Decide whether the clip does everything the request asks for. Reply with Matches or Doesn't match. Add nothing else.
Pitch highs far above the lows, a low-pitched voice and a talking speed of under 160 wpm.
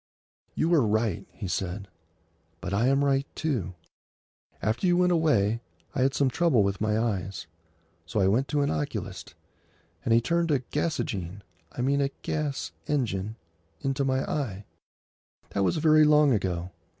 Matches